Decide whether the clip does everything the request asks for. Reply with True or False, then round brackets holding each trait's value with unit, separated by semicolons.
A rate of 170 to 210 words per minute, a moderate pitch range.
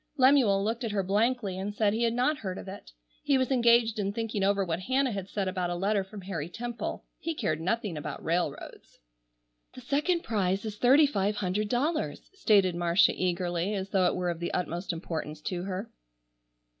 True (195 wpm; 4.4 semitones)